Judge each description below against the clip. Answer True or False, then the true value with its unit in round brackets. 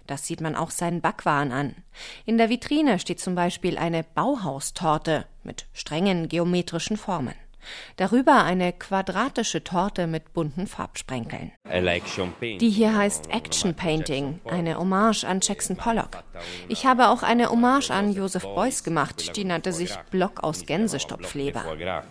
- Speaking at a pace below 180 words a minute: True (140 wpm)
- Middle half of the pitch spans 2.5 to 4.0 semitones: False (4.7 semitones)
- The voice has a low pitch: False (175 Hz)